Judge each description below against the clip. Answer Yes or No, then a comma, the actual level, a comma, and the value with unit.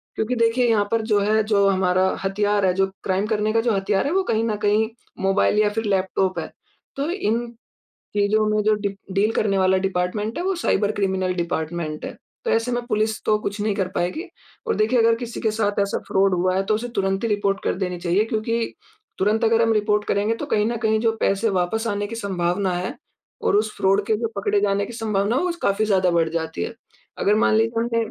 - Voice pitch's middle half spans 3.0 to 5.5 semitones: No, narrow, 2.6 semitones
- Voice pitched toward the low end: No, high, 210 Hz